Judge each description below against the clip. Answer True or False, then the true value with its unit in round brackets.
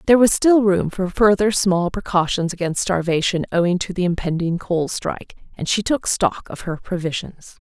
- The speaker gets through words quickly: False (180 wpm)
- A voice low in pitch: False (185 Hz)